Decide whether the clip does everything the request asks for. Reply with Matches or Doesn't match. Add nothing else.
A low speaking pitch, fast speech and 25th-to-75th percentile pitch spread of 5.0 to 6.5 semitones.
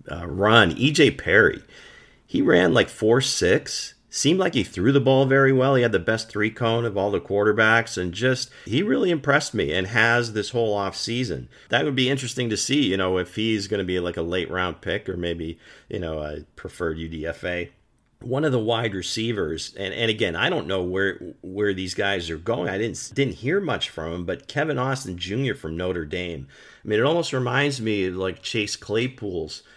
Matches